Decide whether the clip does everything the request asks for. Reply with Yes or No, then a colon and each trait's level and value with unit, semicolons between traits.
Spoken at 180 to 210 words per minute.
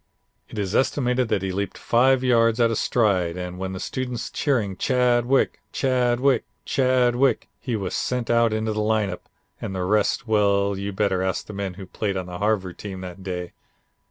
Yes: average, 185 wpm